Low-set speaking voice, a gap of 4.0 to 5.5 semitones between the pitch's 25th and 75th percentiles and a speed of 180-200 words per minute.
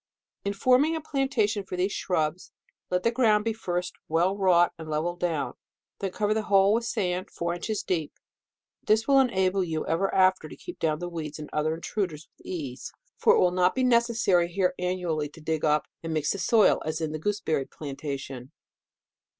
No: medium, 180 Hz; average, 4.7 semitones; average, 190 wpm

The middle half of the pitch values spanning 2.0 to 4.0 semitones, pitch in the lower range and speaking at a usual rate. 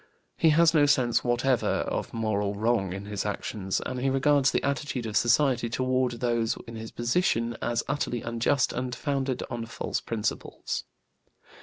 Yes: average, 3.0 semitones; low, 120 Hz; average, 160 wpm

